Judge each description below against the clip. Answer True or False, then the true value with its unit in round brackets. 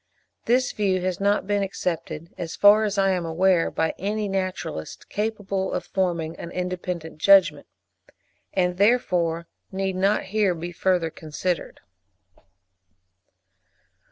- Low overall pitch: False (185 Hz)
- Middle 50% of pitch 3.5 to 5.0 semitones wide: False (2.7 semitones)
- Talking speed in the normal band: False (125 wpm)